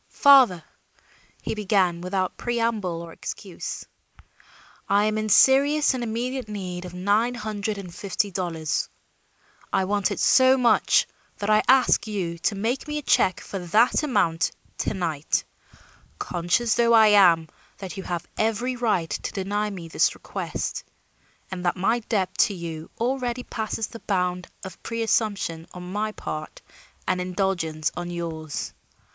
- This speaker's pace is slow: No, average, 150 wpm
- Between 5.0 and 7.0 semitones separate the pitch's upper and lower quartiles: No, average, 4.3 semitones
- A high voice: Yes, high, 200 Hz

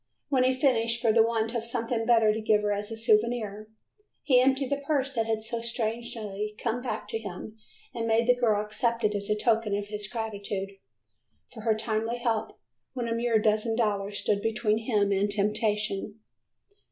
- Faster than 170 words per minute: Yes, average, 190 wpm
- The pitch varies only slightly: Yes, narrow, 1.9 semitones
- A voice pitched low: No, high, 225 Hz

